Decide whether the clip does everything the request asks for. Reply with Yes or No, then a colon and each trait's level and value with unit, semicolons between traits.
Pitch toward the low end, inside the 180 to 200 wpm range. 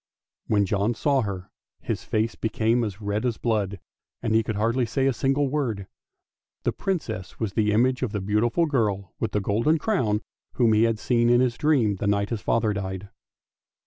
Yes: low, 110 Hz; average, 190 wpm